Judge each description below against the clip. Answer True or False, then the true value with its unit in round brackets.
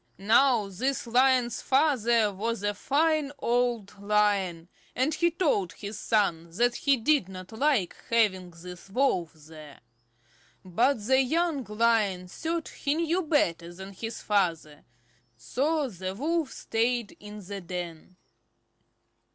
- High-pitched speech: True (220 Hz)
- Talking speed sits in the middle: False (125 wpm)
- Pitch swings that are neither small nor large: False (6.3 semitones)